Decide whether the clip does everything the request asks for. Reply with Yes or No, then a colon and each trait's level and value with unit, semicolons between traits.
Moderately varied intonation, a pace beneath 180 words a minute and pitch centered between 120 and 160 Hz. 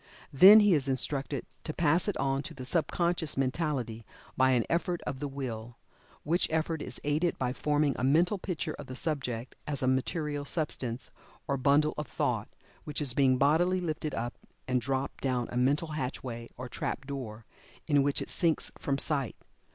No: average, 3.4 semitones; average, 185 wpm; medium, 140 Hz